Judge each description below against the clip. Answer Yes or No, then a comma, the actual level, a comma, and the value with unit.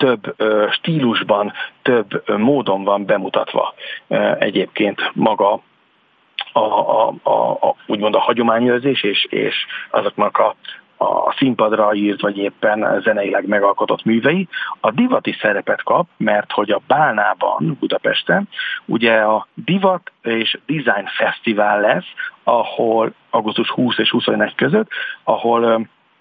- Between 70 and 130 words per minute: Yes, average, 110 wpm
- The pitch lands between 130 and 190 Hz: No, low, 120 Hz